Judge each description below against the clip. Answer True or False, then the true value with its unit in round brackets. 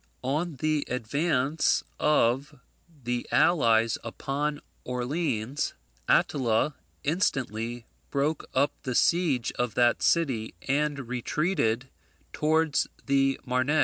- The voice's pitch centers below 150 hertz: True (135 Hz)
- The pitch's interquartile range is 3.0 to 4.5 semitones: True (3.7 semitones)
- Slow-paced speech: True (95 wpm)